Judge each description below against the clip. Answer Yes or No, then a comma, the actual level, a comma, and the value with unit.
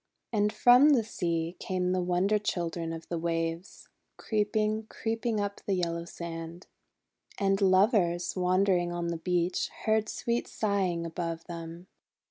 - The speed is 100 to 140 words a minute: Yes, slow, 135 wpm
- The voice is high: No, medium, 180 Hz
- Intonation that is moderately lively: Yes, average, 3.6 semitones